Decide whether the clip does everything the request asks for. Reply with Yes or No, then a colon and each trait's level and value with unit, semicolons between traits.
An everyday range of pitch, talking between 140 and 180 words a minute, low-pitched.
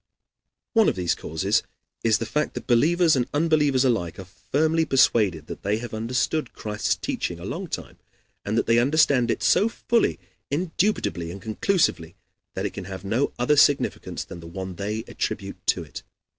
No: wide, 7.6 semitones; average, 175 wpm; low, 120 Hz